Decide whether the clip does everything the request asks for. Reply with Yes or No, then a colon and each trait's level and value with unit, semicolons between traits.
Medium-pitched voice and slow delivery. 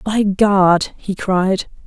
No: high, 195 Hz; slow, 130 wpm